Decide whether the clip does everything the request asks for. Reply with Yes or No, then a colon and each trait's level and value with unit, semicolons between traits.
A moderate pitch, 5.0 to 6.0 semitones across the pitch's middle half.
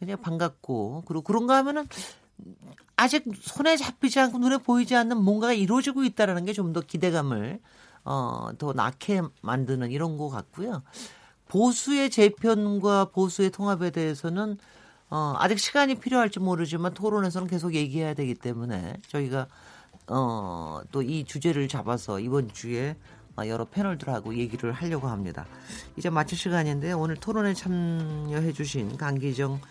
No: medium, 170 Hz; wide, 6.9 semitones